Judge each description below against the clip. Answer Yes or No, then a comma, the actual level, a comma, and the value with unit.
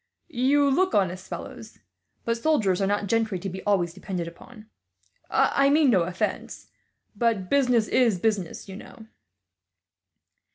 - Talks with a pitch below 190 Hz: No, high, 215 Hz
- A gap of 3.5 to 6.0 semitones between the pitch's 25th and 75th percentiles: Yes, average, 5.0 semitones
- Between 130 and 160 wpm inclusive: Yes, slow, 135 wpm